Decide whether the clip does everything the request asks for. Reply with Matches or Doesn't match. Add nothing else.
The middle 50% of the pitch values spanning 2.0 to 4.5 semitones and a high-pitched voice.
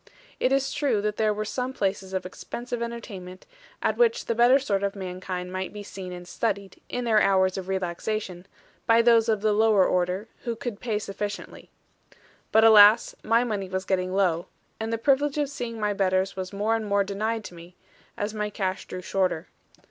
Matches